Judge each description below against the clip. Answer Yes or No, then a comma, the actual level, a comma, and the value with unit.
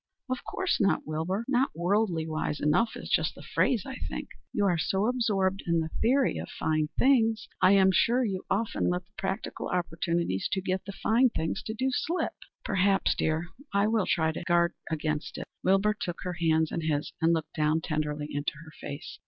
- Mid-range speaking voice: Yes, medium, 180 Hz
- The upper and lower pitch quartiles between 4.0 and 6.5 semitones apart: Yes, average, 5.0 semitones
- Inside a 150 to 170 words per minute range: No, average, 200 wpm